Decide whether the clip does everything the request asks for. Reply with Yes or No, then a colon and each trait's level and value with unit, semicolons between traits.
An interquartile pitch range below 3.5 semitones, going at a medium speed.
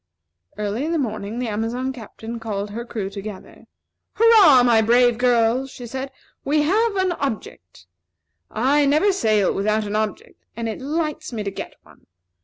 No: average, 4.7 semitones; average, 165 wpm